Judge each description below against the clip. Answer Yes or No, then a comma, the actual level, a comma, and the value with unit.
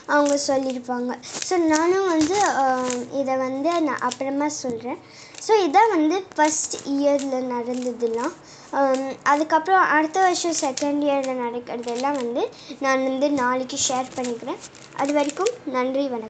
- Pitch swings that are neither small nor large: Yes, average, 3.6 semitones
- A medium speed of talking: Yes, average, 120 wpm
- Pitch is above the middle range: Yes, very high, 275 Hz